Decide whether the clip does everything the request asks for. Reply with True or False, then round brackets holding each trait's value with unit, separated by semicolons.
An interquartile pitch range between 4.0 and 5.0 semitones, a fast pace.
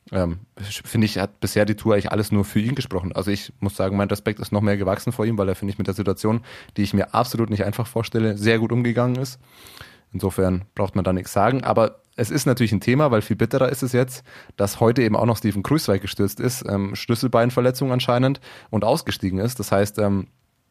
False (3.3 semitones; 230 wpm)